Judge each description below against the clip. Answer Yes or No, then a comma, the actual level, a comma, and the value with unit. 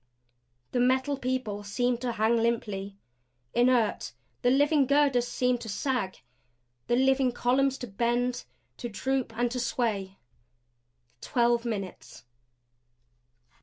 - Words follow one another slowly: Yes, slow, 115 wpm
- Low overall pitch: No, high, 245 Hz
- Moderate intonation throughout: No, narrow, 2.2 semitones